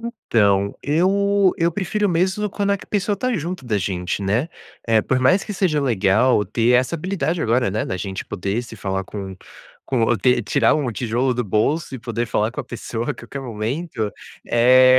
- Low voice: Yes, low, 125 Hz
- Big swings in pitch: Yes, wide, 7.8 semitones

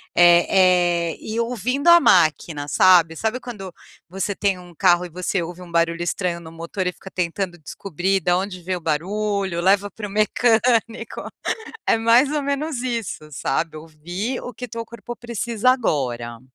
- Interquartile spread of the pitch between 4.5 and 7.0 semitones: Yes, average, 5.0 semitones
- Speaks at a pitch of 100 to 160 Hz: No, medium, 185 Hz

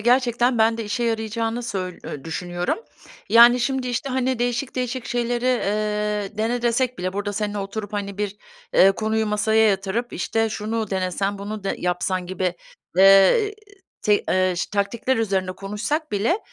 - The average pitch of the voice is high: Yes, high, 215 Hz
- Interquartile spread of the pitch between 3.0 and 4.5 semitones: Yes, average, 3.4 semitones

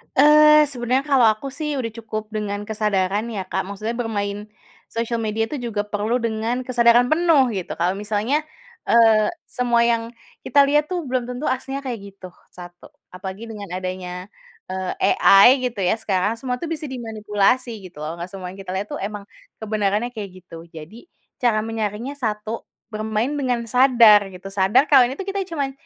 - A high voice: Yes, high, 225 Hz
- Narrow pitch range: No, average, 3.8 semitones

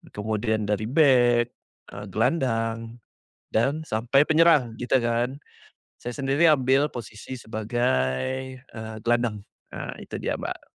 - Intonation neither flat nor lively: Yes, average, 3.2 semitones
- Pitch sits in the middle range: No, low, 120 Hz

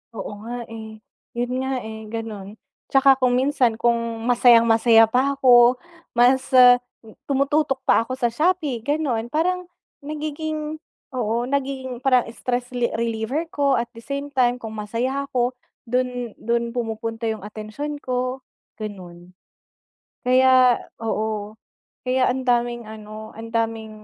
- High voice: Yes, high, 245 Hz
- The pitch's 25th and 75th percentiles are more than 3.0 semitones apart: No, average, 2.7 semitones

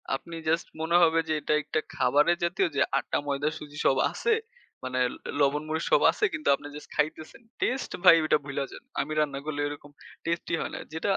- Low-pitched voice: No, medium, 155 Hz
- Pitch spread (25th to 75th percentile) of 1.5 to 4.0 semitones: Yes, narrow, 2.6 semitones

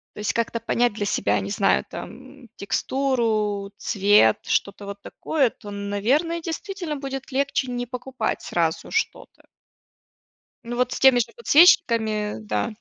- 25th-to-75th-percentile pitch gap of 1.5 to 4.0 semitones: No, average, 4.8 semitones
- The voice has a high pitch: Yes, high, 235 Hz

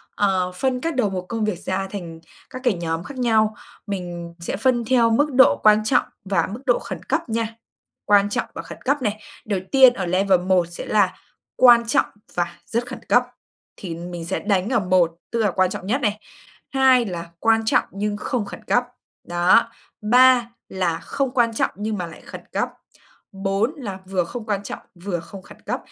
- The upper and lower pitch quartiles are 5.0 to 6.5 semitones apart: No, average, 4.5 semitones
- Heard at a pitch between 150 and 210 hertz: Yes, high, 205 Hz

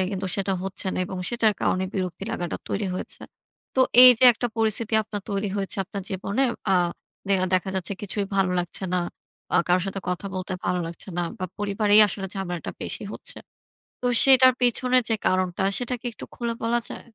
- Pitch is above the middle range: Yes, high, 200 Hz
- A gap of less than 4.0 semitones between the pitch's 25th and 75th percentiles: Yes, average, 3.3 semitones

